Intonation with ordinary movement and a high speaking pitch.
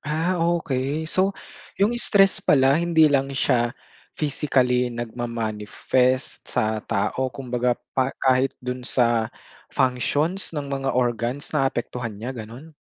No: average, 3.8 semitones; low, 130 Hz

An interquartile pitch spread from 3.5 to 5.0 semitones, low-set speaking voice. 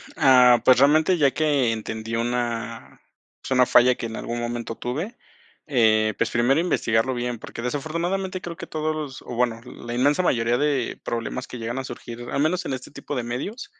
Yes: average, 4.0 semitones; low, 125 Hz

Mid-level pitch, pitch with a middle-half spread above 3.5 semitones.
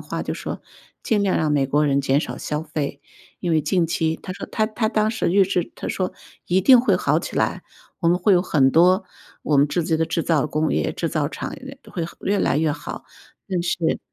Yes: medium, 170 Hz; average, 3.9 semitones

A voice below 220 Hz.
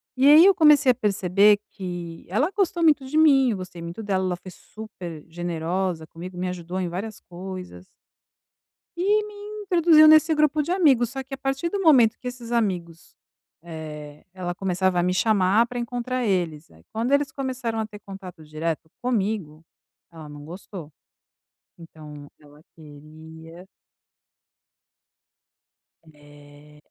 Yes: high, 190 Hz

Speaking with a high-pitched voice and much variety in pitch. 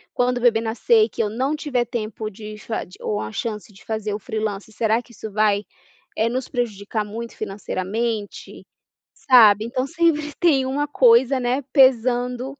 No: high, 230 Hz; average, 3.3 semitones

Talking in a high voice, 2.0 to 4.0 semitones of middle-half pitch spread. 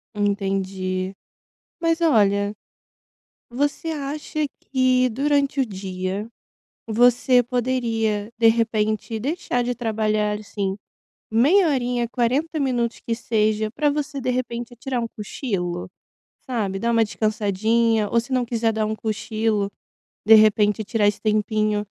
Yes: high, 225 Hz; average, 3.2 semitones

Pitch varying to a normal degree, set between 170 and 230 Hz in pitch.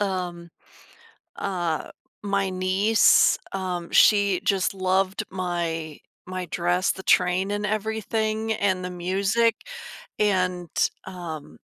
No: narrow, 2.2 semitones; medium, 185 Hz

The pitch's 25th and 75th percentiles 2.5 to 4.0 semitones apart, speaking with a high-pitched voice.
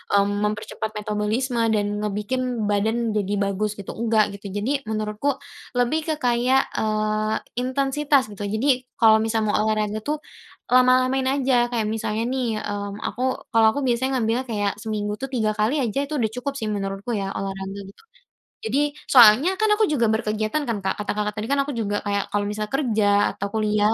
Yes: average, 3.4 semitones; high, 220 Hz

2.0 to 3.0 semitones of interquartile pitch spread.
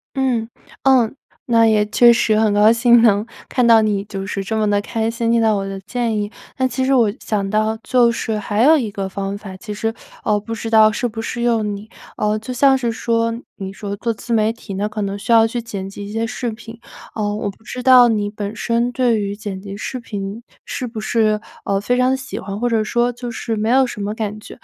Yes: narrow, 2.4 semitones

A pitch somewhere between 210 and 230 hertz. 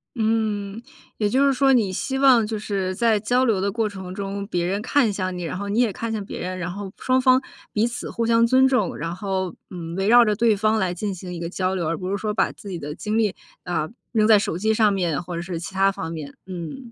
No: high, 200 Hz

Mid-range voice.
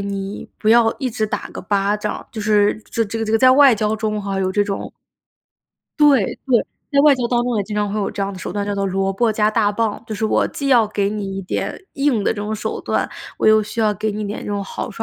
No: high, 215 Hz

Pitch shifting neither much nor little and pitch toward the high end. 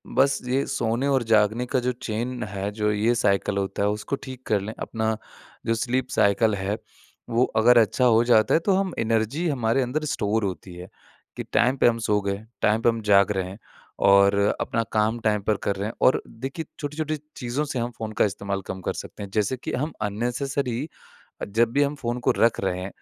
No: average, 3.7 semitones; low, 115 Hz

